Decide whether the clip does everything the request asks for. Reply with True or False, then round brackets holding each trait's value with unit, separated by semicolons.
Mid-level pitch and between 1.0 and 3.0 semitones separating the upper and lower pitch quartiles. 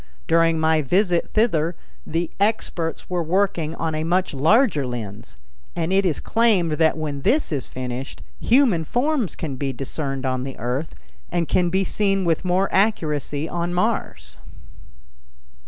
False (165 Hz; 4.6 semitones)